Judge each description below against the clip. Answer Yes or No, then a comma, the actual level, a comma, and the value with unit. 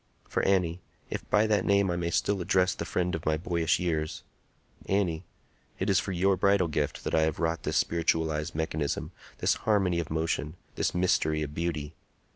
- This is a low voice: Yes, very low, 85 Hz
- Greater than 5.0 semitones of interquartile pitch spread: No, average, 2.9 semitones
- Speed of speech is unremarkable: Yes, average, 175 wpm